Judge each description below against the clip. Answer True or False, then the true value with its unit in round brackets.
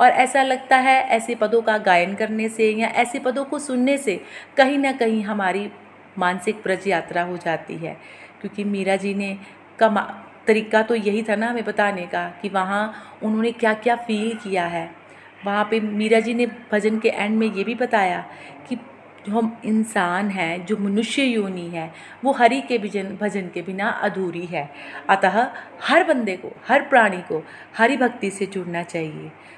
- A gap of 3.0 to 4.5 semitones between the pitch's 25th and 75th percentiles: True (3.4 semitones)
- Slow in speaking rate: False (180 wpm)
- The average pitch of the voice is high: True (215 Hz)